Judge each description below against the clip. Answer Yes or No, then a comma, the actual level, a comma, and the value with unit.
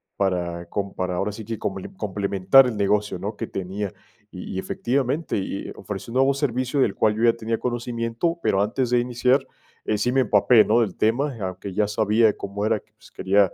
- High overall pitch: No, low, 110 Hz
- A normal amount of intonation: Yes, average, 3.6 semitones